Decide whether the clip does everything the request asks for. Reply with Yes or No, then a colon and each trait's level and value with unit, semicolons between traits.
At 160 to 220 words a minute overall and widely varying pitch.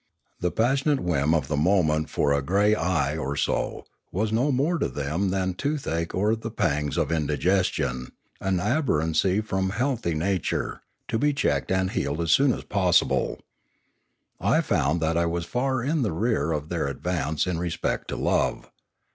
Yes: average, 170 wpm; wide, 6.0 semitones